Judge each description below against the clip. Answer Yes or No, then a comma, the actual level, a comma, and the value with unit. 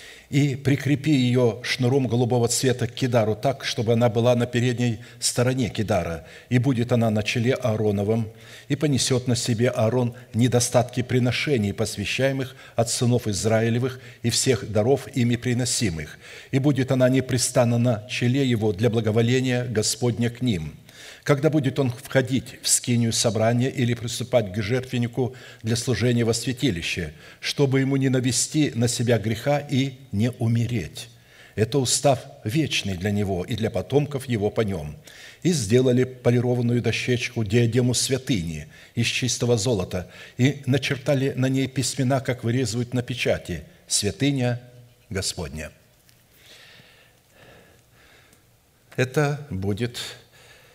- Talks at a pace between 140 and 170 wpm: No, average, 130 wpm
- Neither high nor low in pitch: No, low, 125 Hz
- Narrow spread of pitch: Yes, narrow, 2.2 semitones